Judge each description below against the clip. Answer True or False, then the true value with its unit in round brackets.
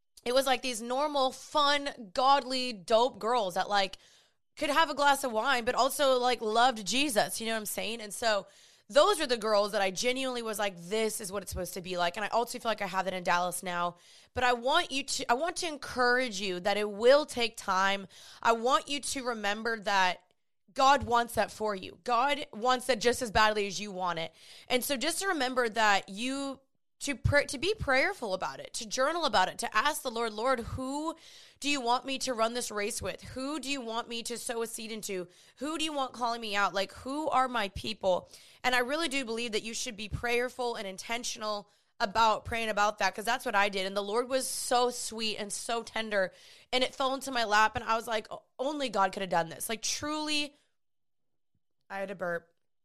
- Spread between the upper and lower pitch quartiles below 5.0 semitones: True (4.2 semitones)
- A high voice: True (235 Hz)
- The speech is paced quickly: True (225 wpm)